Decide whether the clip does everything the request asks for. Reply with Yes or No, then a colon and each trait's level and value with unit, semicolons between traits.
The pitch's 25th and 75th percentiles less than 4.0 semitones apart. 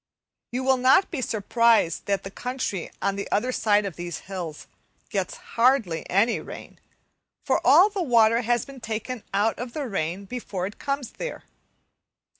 No: average, 4.4 semitones